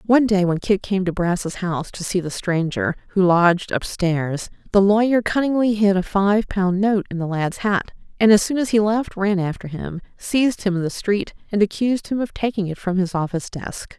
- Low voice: No, high, 195 Hz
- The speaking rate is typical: No, fast, 225 wpm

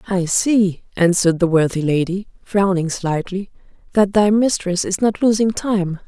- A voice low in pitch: No, high, 190 Hz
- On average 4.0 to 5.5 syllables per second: Yes, 4.5 syllables/s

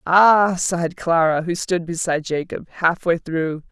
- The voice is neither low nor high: Yes, medium, 170 Hz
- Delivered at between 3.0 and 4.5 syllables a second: Yes, 4.3 syllables/s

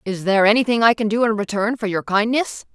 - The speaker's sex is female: Yes, female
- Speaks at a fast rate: Yes, fast, 240 wpm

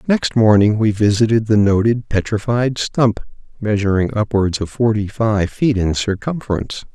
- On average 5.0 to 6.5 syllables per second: No, 4.8 syllables/s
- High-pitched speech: No, low, 110 Hz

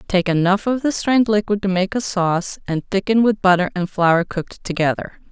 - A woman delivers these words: Yes, female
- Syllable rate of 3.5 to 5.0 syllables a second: No, 5.5 syllables/s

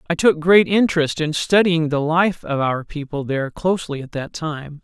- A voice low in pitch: No, medium, 160 Hz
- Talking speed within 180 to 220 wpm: Yes, average, 200 wpm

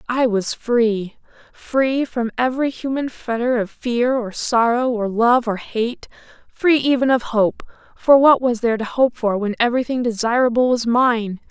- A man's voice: No, female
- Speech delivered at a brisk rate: No, average, 155 wpm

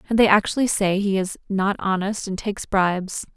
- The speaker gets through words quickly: No, average, 195 wpm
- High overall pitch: Yes, high, 195 Hz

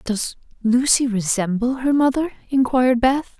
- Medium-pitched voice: No, high, 245 Hz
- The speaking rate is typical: No, slow, 125 wpm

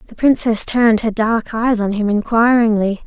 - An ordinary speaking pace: Yes, average, 175 wpm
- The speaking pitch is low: No, high, 225 Hz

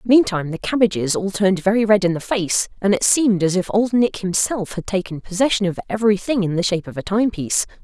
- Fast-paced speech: Yes, fast, 230 wpm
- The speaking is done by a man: No, female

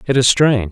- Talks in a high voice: No, low, 120 Hz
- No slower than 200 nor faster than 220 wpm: No, fast, 250 wpm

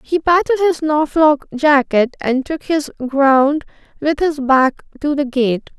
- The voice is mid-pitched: No, very high, 290 Hz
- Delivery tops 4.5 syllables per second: No, 3.9 syllables/s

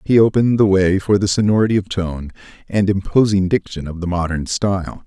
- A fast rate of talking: No, average, 190 wpm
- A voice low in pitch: Yes, very low, 95 Hz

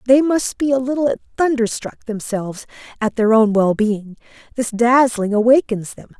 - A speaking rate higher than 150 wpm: No, average, 145 wpm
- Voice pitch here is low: No, high, 235 Hz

